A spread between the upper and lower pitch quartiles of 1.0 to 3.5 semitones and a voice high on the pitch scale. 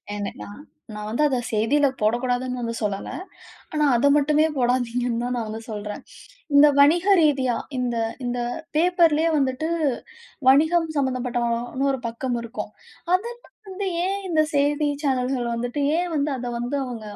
No: average, 3.9 semitones; very high, 255 Hz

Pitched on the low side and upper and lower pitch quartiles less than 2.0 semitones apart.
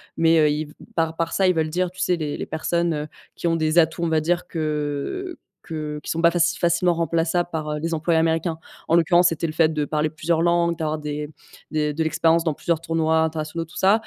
No: medium, 165 Hz; narrow, 1.6 semitones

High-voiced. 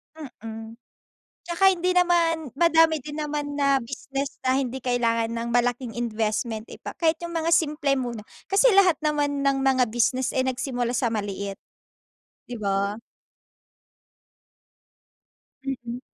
Yes: very high, 265 Hz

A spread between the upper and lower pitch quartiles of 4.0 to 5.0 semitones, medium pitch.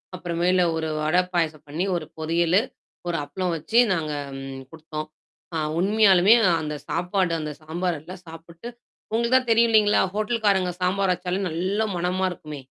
No: average, 3.3 semitones; medium, 180 Hz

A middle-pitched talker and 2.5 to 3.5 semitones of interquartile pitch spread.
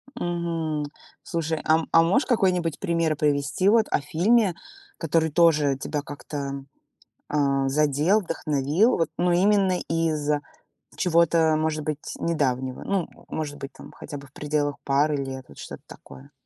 Yes: medium, 155 Hz; average, 2.9 semitones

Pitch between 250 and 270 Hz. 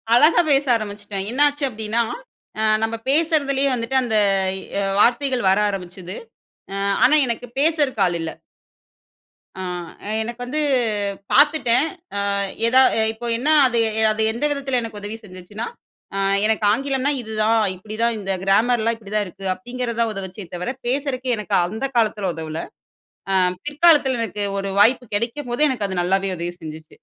No: high, 230 Hz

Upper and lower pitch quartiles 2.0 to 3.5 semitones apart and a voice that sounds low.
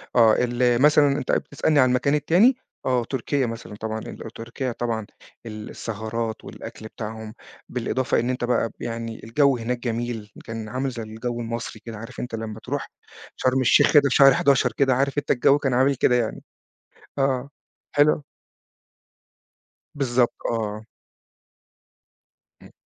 Yes: average, 2.8 semitones; low, 120 Hz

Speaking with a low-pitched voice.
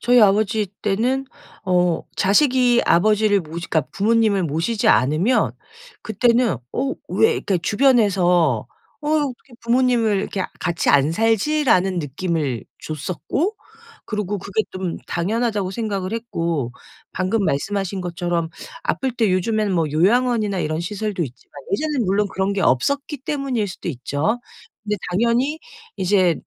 No: high, 205 Hz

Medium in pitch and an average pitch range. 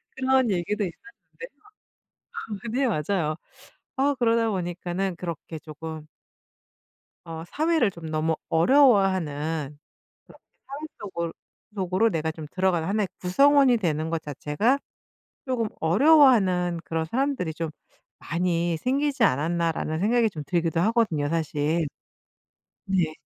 No: medium, 175 Hz; wide, 6.0 semitones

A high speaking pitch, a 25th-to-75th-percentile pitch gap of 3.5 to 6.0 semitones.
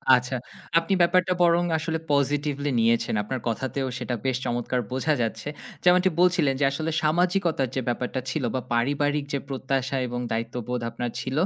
No: low, 135 Hz; average, 4.2 semitones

